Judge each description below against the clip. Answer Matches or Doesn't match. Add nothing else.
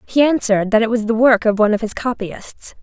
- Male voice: Doesn't match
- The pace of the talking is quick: Matches